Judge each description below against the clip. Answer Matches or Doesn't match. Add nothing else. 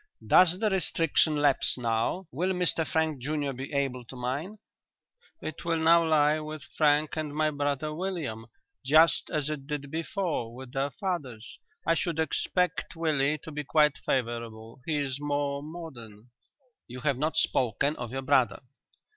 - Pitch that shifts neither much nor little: Matches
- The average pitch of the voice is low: Doesn't match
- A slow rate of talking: Doesn't match